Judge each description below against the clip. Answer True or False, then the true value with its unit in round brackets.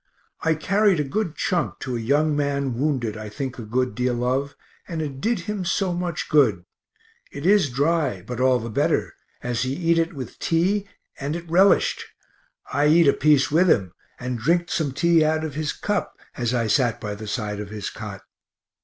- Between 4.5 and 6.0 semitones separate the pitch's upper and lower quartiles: True (5.3 semitones)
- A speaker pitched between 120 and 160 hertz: True (140 Hz)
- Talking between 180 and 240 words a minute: True (195 wpm)